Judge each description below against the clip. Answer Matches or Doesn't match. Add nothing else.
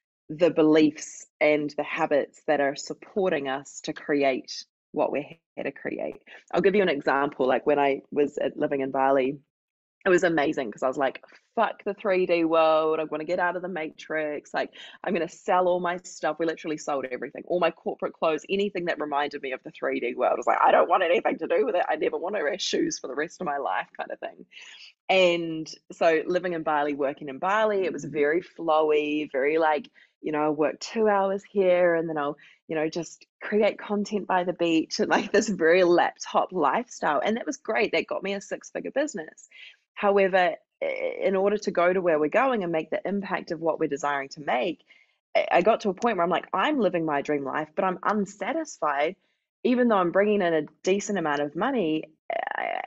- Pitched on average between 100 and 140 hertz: Doesn't match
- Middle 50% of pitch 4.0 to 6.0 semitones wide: Matches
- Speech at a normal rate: Doesn't match